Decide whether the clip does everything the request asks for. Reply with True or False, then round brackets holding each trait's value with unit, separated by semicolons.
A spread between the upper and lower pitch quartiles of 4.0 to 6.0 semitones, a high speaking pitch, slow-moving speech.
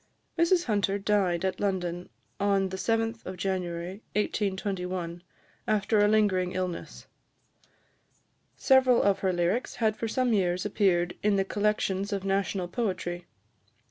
False (2.6 semitones; 195 Hz; 125 wpm)